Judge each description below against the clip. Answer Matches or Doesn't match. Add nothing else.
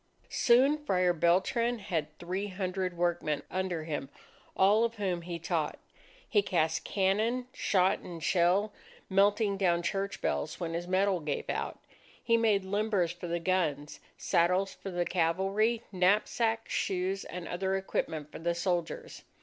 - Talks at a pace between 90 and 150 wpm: Matches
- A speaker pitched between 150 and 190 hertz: Matches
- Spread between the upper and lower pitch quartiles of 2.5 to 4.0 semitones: Matches